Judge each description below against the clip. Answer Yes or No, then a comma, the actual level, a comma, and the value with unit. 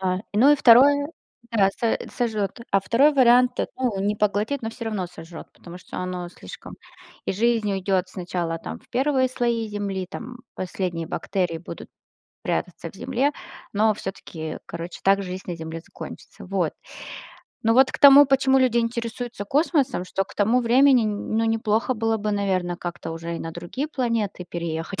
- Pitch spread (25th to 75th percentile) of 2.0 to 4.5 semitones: No, average, 5.0 semitones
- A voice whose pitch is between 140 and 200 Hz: No, high, 210 Hz